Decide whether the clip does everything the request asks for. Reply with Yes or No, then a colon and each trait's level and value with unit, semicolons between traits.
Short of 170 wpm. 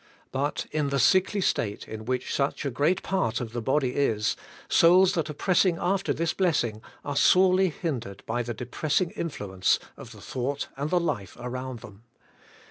No: average, 175 wpm